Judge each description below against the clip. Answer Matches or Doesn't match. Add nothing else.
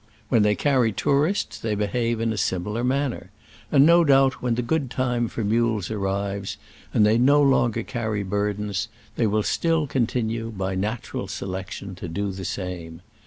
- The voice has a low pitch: Matches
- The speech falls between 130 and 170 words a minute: Matches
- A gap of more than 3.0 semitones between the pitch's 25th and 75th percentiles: Matches